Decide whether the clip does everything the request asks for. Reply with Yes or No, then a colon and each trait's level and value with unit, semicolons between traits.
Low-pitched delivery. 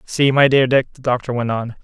Yes: low, 130 Hz